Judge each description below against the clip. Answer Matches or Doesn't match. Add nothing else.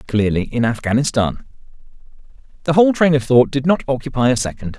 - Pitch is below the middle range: Matches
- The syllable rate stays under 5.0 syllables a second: Doesn't match